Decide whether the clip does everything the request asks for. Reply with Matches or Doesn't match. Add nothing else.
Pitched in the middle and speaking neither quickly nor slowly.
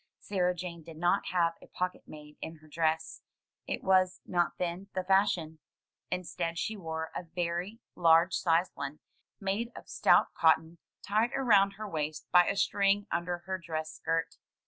Matches